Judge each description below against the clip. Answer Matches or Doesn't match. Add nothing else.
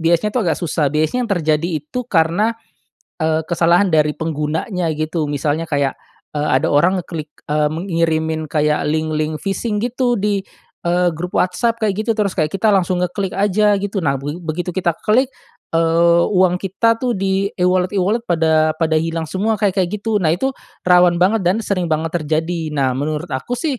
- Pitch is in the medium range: Matches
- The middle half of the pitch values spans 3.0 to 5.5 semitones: Matches